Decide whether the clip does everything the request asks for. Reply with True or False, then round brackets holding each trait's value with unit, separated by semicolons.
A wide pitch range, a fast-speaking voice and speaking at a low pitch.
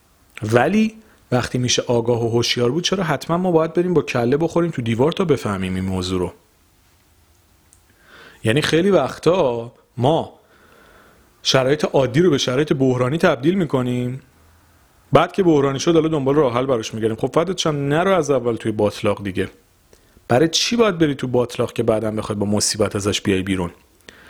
True (7.4 semitones; 165 wpm; 120 Hz)